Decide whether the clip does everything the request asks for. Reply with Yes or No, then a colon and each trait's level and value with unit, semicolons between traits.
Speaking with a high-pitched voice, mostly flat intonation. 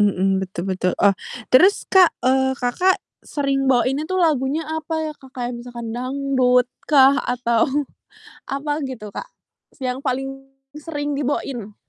No: very high, 265 Hz; average, 3.2 semitones